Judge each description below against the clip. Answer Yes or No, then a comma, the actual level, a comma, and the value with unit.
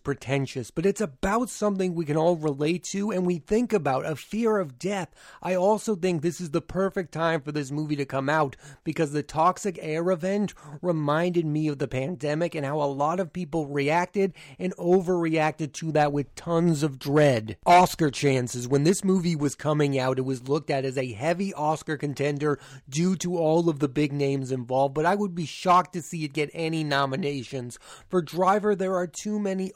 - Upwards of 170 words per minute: Yes, average, 200 wpm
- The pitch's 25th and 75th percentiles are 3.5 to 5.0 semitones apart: Yes, average, 4.1 semitones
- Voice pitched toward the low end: No, medium, 160 Hz